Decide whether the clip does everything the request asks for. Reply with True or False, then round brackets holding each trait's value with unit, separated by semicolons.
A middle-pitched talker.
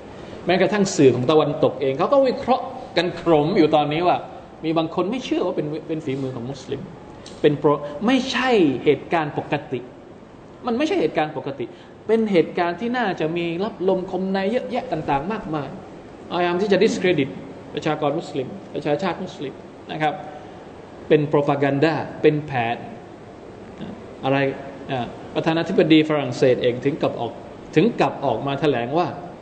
True (160 Hz)